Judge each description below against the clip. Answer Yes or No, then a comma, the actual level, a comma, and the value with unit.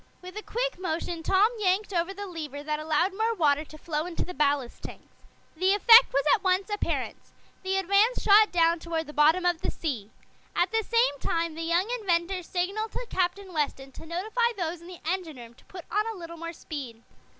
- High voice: Yes, very high, 350 Hz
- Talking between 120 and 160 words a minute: No, fast, 205 wpm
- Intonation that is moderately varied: Yes, average, 3.9 semitones